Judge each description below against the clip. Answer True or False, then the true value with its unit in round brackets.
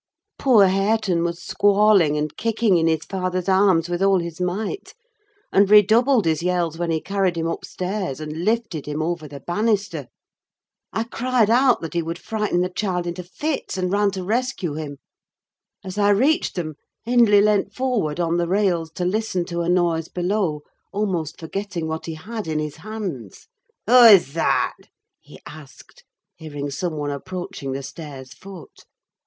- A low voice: False (180 Hz)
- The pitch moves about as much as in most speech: True (4.3 semitones)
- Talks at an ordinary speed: True (165 wpm)